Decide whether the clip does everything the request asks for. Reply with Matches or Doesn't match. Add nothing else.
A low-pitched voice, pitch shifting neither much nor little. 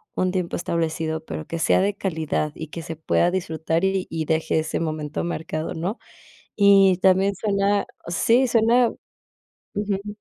Doesn't match